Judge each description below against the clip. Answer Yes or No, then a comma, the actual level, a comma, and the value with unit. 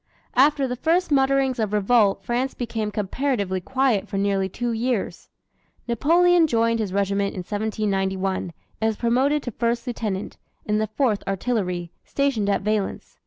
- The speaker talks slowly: No, average, 150 wpm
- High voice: Yes, high, 220 Hz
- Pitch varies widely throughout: No, average, 4.4 semitones